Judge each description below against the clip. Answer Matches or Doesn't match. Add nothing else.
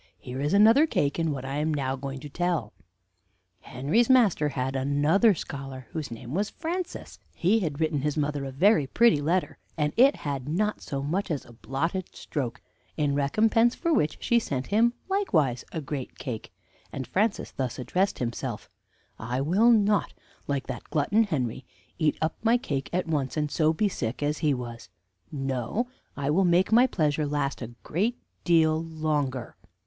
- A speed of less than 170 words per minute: Doesn't match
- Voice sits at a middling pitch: Matches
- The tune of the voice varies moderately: Doesn't match